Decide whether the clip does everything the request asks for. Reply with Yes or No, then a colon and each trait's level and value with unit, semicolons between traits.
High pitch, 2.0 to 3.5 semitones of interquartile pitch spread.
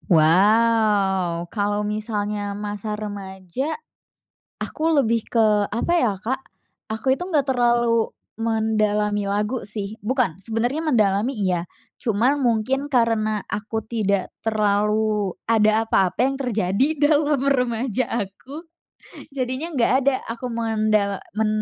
Yes: high, 220 Hz; average, 2.9 semitones